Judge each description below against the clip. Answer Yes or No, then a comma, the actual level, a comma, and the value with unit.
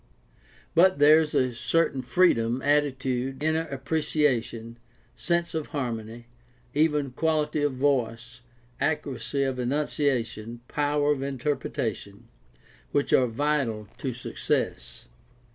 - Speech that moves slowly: Yes, slow, 110 wpm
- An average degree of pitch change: Yes, average, 3.7 semitones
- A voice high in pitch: No, low, 135 Hz